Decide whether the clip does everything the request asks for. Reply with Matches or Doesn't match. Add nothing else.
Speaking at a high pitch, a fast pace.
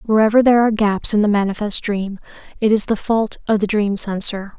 Matches